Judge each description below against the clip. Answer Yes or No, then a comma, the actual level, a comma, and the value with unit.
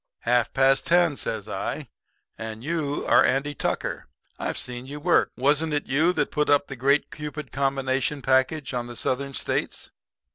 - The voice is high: No, medium, 140 Hz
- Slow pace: No, average, 170 wpm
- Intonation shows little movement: Yes, narrow, 2.3 semitones